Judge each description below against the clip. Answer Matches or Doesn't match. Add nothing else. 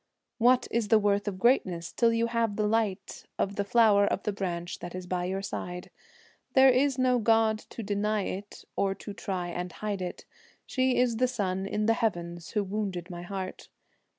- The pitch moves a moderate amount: Matches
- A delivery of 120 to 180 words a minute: Doesn't match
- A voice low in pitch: Doesn't match